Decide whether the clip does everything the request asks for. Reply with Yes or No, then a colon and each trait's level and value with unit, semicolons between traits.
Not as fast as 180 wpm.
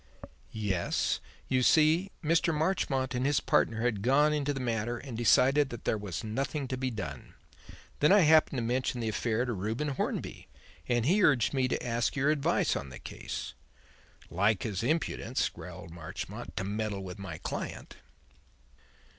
Yes: average, 165 wpm